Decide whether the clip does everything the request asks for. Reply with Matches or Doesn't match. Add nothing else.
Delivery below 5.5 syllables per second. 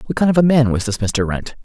Doesn't match